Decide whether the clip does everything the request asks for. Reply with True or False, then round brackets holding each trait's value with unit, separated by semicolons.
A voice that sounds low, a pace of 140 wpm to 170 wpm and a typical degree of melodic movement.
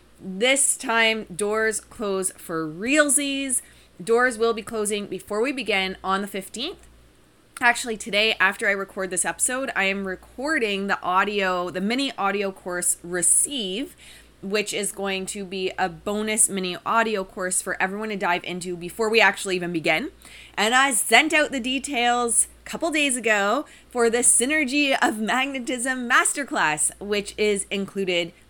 False (210 Hz; 150 wpm; 4.4 semitones)